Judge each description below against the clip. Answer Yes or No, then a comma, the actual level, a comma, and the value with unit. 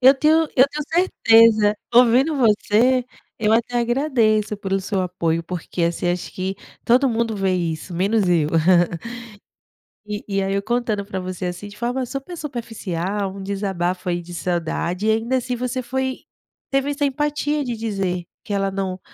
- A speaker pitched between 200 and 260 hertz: Yes, high, 215 Hz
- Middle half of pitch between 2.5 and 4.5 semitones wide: No, average, 5.1 semitones